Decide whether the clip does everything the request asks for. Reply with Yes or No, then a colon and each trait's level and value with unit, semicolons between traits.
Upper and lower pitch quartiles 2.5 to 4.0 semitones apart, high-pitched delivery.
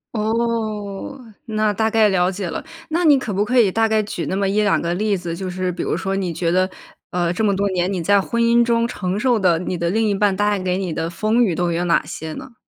Yes: average, 3.4 semitones; high, 200 Hz